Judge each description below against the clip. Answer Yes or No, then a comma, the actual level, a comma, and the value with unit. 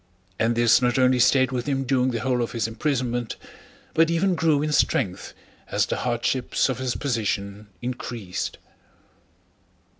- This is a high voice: No, low, 125 Hz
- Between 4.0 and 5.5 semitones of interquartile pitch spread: No, narrow, 2.5 semitones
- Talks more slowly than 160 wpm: Yes, average, 150 wpm